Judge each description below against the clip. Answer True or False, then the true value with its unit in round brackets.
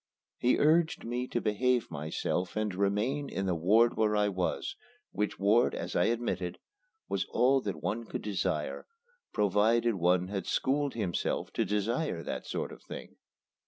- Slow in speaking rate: False (160 wpm)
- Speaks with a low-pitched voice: True (105 Hz)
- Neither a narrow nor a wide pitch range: True (4.4 semitones)